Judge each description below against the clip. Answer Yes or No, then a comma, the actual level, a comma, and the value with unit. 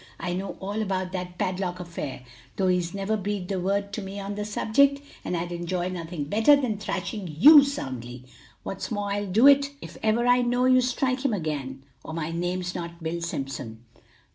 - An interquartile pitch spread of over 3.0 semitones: Yes, average, 4.2 semitones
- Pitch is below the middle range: No, high, 190 Hz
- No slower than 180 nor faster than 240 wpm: Yes, average, 195 wpm